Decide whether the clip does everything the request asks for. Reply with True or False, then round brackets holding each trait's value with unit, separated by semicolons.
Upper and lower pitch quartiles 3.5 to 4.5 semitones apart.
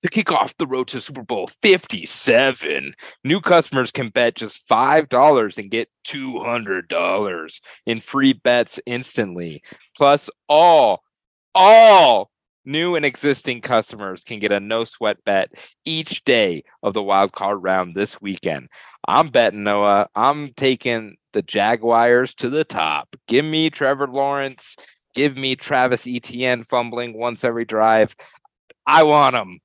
True (4.1 semitones)